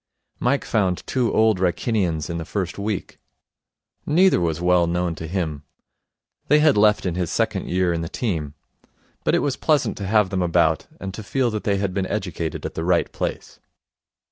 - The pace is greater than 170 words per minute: Yes, average, 190 wpm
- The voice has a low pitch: Yes, very low, 95 Hz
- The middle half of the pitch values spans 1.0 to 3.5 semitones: No, average, 4.1 semitones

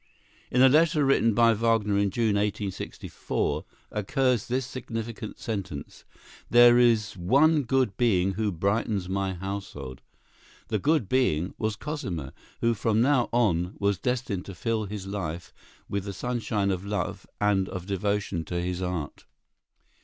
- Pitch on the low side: Yes, low, 105 Hz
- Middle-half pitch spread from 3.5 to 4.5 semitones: Yes, average, 4.0 semitones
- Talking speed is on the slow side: No, average, 145 wpm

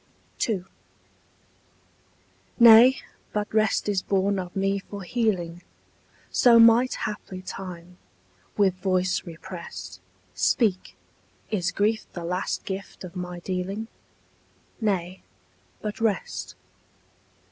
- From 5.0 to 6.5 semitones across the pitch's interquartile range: No, average, 2.9 semitones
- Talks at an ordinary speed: No, slow, 100 wpm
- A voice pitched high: Yes, high, 195 Hz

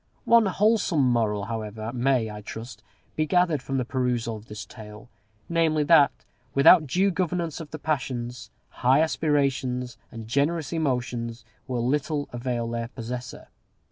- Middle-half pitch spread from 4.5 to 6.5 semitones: Yes, average, 4.9 semitones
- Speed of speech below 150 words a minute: Yes, average, 140 wpm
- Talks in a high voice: No, low, 130 Hz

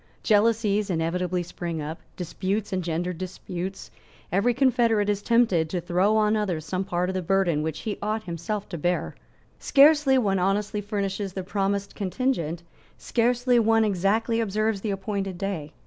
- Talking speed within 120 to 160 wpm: Yes, average, 150 wpm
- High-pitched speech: Yes, high, 195 Hz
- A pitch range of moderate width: Yes, average, 3.3 semitones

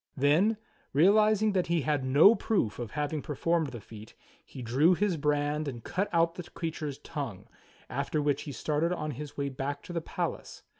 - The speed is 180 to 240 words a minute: Yes, average, 185 wpm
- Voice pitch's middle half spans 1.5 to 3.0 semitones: No, average, 3.5 semitones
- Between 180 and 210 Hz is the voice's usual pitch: No, medium, 150 Hz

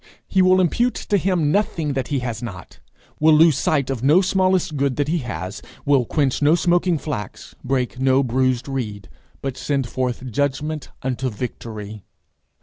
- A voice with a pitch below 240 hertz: Yes, low, 135 Hz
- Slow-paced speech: No, average, 165 wpm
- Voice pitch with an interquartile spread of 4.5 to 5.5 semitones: No, average, 4.1 semitones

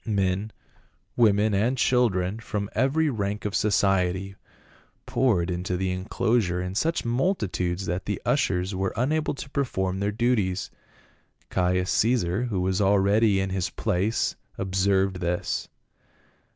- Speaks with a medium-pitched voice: No, low, 100 Hz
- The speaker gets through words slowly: Yes, slow, 125 wpm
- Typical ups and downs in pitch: Yes, average, 3.7 semitones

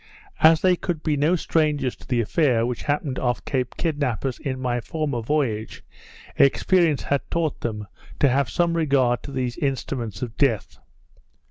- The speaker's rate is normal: Yes, average, 160 wpm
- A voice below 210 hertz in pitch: Yes, low, 135 Hz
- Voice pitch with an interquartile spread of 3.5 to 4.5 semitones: Yes, average, 4.0 semitones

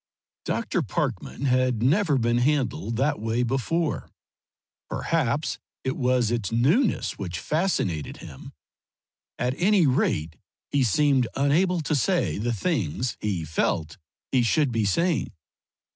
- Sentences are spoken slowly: Yes, slow, 125 wpm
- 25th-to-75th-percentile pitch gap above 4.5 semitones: Yes, average, 5.1 semitones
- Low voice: Yes, low, 130 Hz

